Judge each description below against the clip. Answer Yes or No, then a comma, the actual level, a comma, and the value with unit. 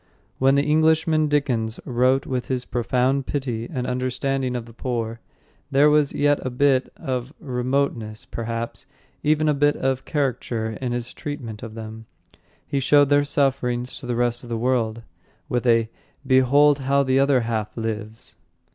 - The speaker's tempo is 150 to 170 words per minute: Yes, average, 160 wpm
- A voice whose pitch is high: No, low, 130 Hz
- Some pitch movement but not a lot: Yes, average, 3.1 semitones